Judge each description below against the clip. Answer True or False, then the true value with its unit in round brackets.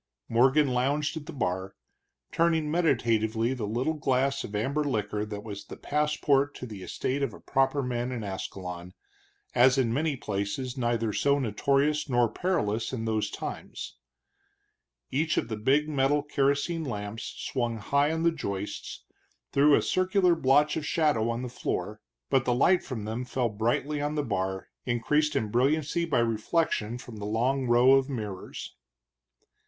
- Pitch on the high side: False (130 Hz)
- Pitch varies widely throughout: False (4.7 semitones)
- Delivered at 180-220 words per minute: False (160 wpm)